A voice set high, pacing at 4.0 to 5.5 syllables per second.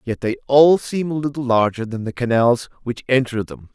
No: low, 125 Hz; 5.2 syllables/s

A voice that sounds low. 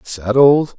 Yes: low, 125 Hz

